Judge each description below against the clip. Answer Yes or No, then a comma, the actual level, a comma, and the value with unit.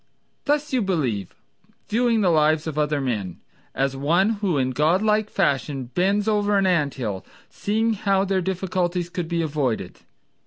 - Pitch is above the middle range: No, medium, 175 Hz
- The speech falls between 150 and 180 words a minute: Yes, average, 155 wpm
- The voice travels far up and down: Yes, wide, 6.1 semitones